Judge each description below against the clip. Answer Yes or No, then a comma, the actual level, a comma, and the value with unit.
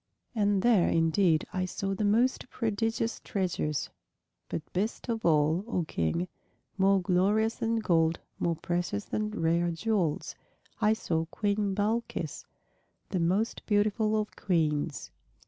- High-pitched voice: Yes, high, 195 Hz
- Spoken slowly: Yes, slow, 130 wpm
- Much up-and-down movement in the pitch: No, average, 4.4 semitones